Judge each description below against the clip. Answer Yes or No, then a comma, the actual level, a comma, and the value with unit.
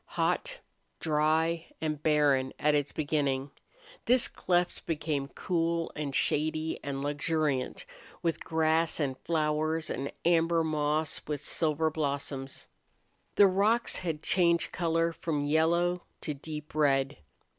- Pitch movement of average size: No, narrow, 2.2 semitones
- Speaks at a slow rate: Yes, slow, 120 wpm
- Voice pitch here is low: No, medium, 155 Hz